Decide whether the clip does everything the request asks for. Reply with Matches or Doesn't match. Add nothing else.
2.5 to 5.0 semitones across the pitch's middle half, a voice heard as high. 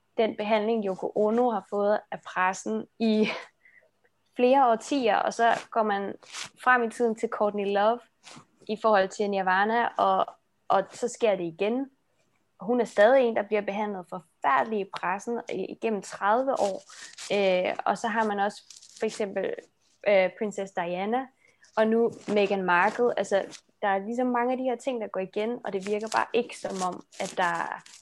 Matches